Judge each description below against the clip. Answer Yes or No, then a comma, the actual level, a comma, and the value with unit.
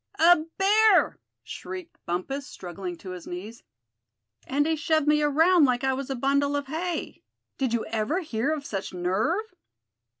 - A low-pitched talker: No, very high, 280 Hz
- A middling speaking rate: Yes, average, 160 wpm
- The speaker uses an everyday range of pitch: No, wide, 6.5 semitones